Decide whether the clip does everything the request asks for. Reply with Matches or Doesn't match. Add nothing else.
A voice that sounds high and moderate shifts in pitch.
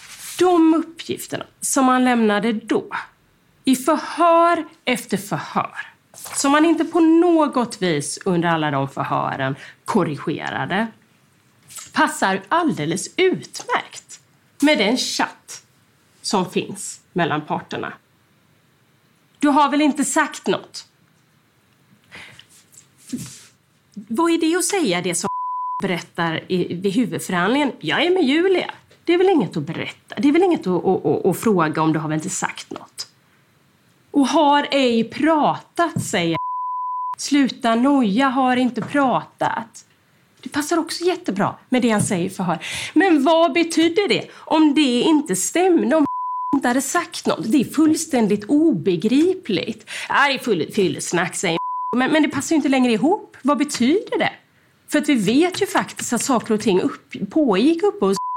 Doesn't match